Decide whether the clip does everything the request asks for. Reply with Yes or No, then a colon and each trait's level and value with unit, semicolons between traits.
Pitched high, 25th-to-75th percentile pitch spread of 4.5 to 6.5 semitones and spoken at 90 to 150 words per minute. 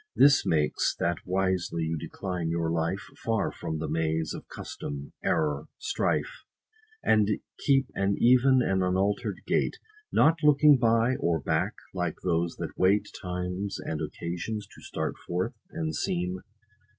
No: very low, 90 Hz; average, 4.8 semitones; average, 145 wpm